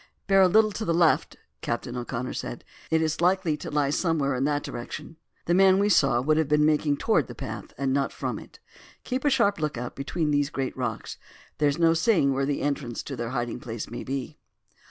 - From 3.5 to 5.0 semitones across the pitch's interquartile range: Yes, average, 4.1 semitones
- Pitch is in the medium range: Yes, medium, 145 Hz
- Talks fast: Yes, fast, 220 wpm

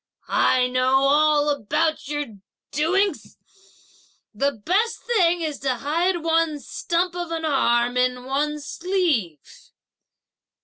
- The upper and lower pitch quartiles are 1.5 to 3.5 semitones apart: No, average, 4.5 semitones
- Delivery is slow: Yes, slow, 115 wpm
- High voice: Yes, very high, 300 Hz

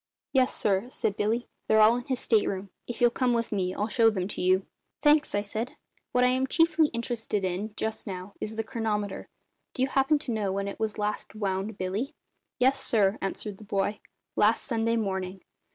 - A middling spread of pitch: Yes, average, 3.6 semitones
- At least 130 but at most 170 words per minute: No, average, 200 wpm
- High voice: Yes, high, 220 Hz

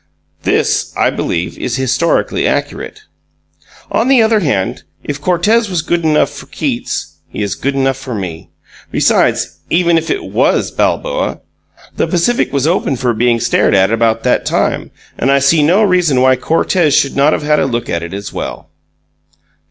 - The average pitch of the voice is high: No, medium, 140 Hz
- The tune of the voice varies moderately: No, wide, 6.2 semitones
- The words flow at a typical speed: Yes, average, 175 wpm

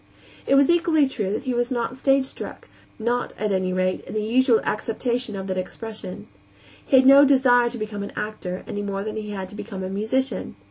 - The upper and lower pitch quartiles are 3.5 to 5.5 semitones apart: Yes, average, 4.3 semitones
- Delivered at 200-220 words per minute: Yes, fast, 205 wpm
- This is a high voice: Yes, high, 220 Hz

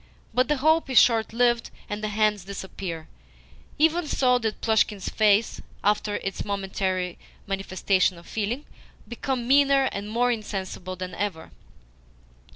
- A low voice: No, high, 210 Hz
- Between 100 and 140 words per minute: Yes, slow, 135 wpm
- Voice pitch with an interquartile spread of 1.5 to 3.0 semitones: No, average, 4.1 semitones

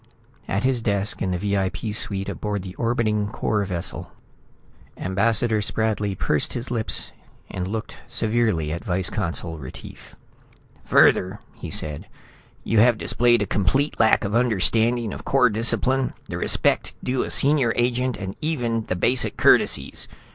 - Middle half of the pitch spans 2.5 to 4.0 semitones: Yes, average, 3.6 semitones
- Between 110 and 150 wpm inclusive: Yes, average, 140 wpm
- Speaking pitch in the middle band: No, low, 110 Hz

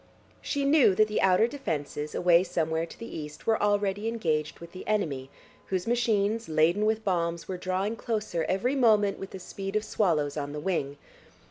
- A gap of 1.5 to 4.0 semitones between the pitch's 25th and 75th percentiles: No, average, 4.7 semitones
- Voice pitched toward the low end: No, high, 190 Hz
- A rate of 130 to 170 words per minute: No, average, 185 wpm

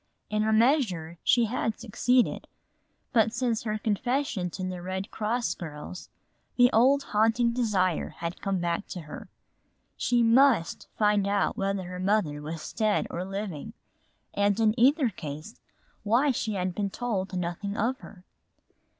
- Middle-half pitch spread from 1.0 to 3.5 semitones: No, average, 4.2 semitones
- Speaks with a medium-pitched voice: No, high, 210 Hz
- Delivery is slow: No, average, 150 wpm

